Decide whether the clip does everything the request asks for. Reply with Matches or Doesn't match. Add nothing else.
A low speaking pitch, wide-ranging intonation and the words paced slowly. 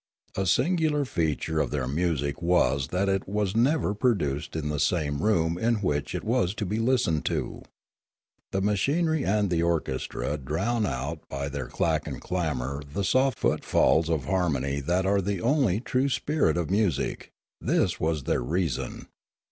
Doesn't match